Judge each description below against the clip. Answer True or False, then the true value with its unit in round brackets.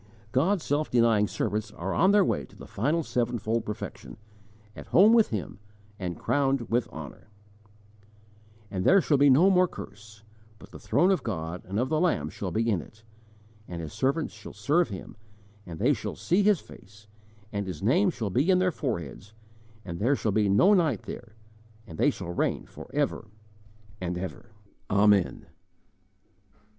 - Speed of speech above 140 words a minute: True (170 wpm)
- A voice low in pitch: True (110 Hz)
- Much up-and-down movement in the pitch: True (7.9 semitones)